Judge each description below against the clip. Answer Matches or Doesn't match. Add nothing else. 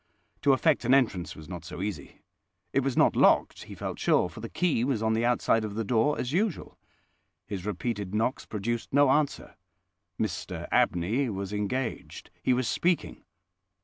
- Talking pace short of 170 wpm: Doesn't match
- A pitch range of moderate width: Matches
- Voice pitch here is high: Doesn't match